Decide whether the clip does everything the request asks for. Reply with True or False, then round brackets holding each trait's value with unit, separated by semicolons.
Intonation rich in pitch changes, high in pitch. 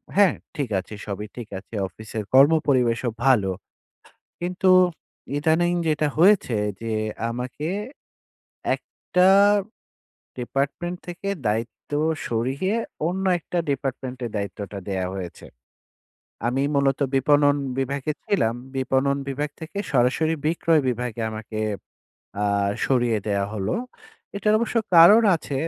False (5.8 semitones; 135 Hz)